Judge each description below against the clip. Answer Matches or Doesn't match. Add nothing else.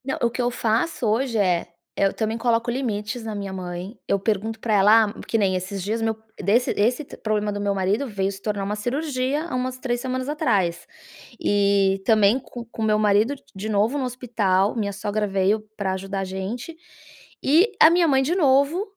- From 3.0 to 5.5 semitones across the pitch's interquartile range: Matches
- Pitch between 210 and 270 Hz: Matches